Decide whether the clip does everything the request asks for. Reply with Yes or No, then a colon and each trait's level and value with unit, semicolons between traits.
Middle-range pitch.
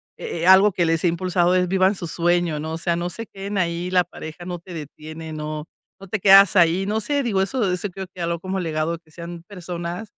Yes: medium, 175 Hz